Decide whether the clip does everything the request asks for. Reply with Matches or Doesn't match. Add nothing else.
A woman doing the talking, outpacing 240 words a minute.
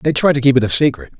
Doesn't match